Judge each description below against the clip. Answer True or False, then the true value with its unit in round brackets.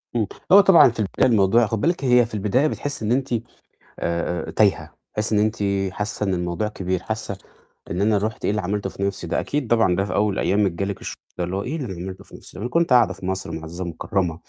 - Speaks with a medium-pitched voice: False (105 Hz)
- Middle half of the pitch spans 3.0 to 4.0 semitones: True (3.4 semitones)